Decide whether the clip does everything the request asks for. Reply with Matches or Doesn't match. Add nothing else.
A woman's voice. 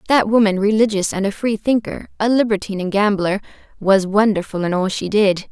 Matches